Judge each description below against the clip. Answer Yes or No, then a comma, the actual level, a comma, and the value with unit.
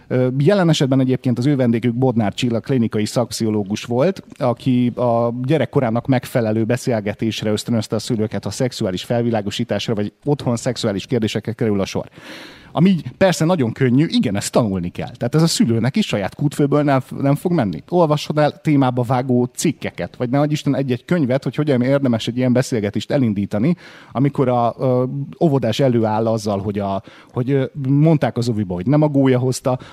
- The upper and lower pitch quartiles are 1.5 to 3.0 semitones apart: No, average, 3.9 semitones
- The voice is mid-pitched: No, low, 125 Hz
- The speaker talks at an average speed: No, fast, 160 wpm